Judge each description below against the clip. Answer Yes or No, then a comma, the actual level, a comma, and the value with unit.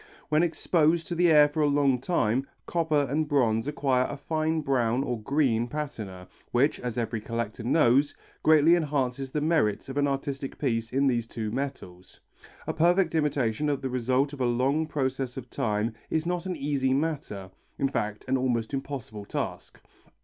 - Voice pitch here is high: No, low, 135 Hz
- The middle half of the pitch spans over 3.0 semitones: Yes, average, 4.0 semitones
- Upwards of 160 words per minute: Yes, average, 175 wpm